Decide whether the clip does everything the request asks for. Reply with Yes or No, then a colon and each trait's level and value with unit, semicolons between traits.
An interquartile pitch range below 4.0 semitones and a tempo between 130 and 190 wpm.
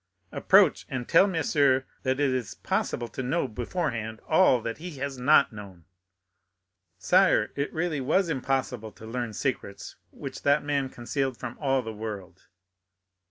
No: average, 4.3 semitones; average, 150 wpm